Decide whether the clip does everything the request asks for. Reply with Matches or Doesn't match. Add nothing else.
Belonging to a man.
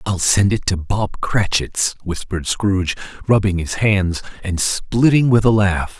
Matches